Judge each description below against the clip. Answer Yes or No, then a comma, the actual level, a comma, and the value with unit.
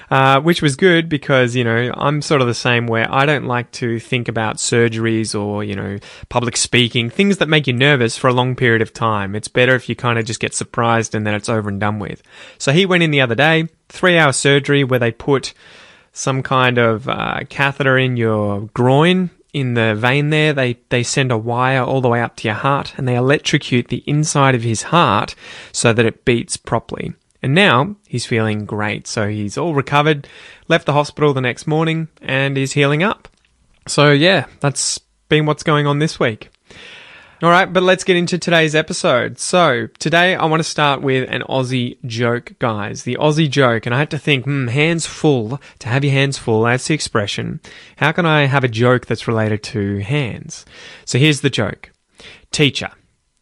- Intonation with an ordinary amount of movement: Yes, average, 4.2 semitones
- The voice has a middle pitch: No, low, 130 Hz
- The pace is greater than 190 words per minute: Yes, fast, 205 wpm